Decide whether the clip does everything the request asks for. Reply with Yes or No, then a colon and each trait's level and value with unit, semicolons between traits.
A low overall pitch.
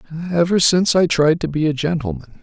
No: medium, 155 Hz